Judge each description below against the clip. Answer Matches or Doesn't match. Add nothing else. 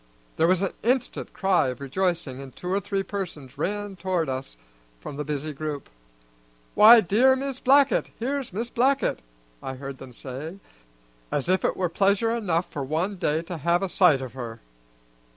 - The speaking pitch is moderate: Matches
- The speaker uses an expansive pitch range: Matches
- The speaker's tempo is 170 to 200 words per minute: Matches